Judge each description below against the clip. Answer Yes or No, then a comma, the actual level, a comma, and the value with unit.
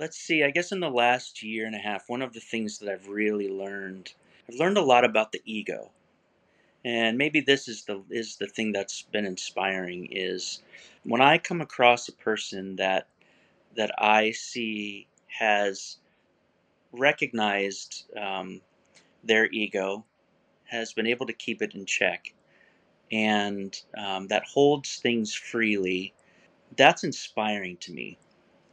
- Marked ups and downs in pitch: No, average, 3.3 semitones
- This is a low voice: Yes, low, 110 Hz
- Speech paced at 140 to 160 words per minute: Yes, average, 150 wpm